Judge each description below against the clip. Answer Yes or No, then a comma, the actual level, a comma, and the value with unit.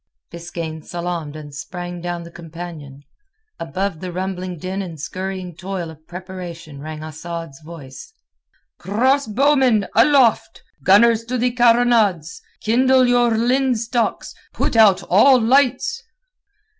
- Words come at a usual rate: No, slow, 115 wpm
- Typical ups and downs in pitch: No, wide, 5.9 semitones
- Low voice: No, medium, 185 Hz